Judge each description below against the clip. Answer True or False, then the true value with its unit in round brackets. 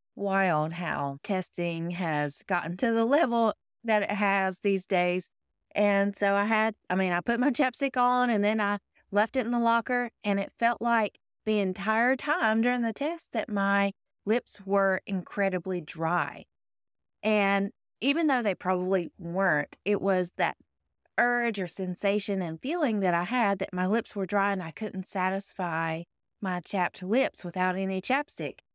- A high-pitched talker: True (200 Hz)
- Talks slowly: False (165 wpm)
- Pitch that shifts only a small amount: False (3.8 semitones)